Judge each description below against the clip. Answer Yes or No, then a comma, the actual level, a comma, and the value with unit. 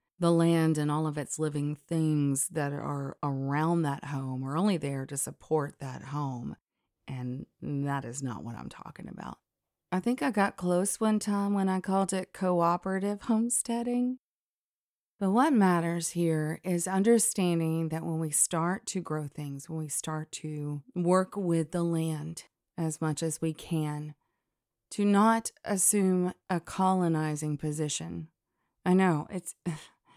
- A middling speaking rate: Yes, average, 150 wpm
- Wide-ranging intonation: No, average, 4.0 semitones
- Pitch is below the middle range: No, medium, 165 Hz